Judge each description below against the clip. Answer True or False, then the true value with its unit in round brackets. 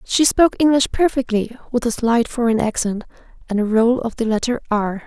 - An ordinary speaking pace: True (190 wpm)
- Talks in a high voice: True (235 Hz)